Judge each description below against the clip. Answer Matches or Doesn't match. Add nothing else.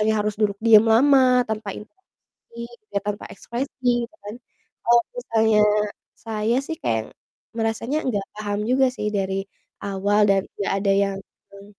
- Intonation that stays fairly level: Doesn't match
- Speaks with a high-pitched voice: Matches